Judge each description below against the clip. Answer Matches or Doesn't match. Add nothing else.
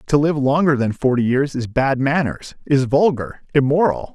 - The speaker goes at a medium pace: Matches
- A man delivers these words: Matches